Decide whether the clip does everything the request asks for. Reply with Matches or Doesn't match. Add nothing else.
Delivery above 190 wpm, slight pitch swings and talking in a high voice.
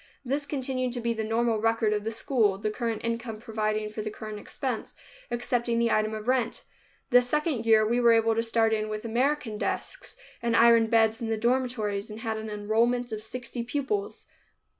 Matches